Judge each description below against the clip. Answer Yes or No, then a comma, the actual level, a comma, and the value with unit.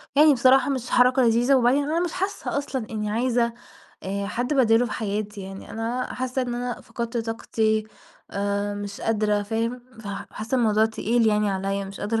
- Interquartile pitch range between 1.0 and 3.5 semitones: Yes, average, 3.2 semitones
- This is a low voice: No, high, 225 Hz